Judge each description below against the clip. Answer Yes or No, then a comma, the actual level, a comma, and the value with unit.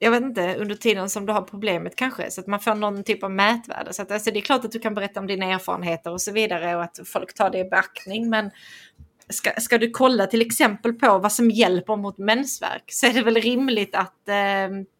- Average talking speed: No, fast, 245 wpm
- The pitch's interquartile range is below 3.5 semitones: Yes, average, 3.0 semitones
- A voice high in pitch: Yes, high, 210 Hz